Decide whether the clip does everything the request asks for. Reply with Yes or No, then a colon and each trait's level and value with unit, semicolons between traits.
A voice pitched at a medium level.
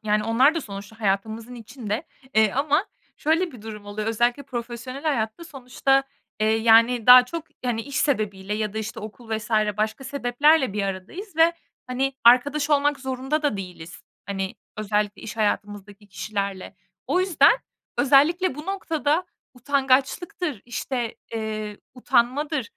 No: high, 240 Hz